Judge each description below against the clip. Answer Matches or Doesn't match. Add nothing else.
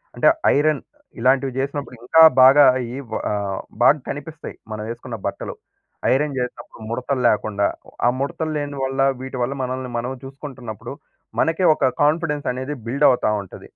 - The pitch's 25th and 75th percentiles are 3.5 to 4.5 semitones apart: Doesn't match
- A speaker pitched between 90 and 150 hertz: Matches